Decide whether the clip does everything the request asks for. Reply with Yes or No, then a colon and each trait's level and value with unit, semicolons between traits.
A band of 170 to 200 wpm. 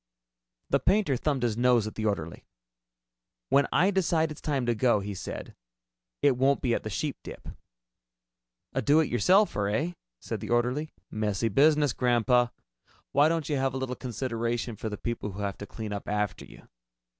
Yes: average, 180 wpm